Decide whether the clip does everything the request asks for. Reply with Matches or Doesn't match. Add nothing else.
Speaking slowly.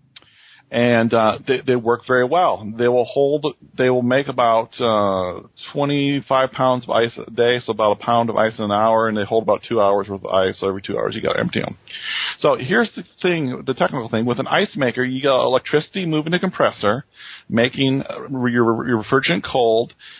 Doesn't match